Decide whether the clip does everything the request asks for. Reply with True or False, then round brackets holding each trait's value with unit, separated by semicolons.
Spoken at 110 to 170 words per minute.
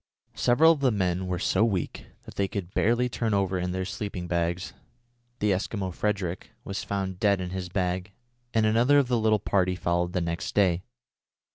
False (185 wpm)